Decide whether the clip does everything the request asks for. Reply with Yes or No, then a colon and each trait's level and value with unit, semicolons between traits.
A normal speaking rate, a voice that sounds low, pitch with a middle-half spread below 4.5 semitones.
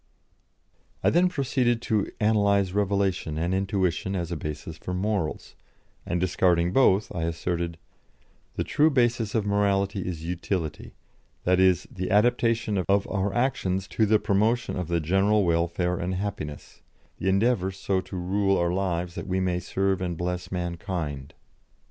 Yes: average, 150 wpm; very low, 95 Hz; average, 2.7 semitones